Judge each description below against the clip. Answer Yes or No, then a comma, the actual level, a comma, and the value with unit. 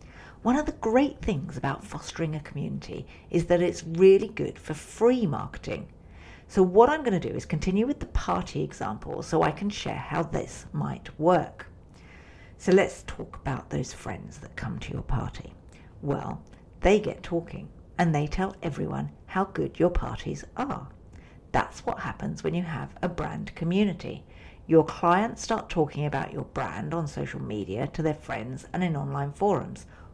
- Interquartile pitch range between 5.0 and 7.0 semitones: Yes, wide, 5.5 semitones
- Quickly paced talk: No, average, 175 wpm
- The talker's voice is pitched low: No, medium, 165 Hz